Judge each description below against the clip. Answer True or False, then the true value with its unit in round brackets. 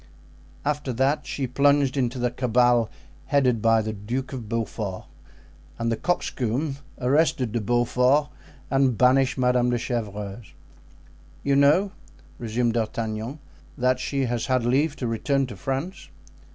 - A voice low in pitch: True (125 Hz)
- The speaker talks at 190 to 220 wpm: False (135 wpm)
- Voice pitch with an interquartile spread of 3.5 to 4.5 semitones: False (2.9 semitones)